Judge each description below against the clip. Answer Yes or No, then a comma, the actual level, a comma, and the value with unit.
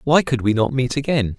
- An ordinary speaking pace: No, fast, 260 wpm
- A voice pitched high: No, low, 130 Hz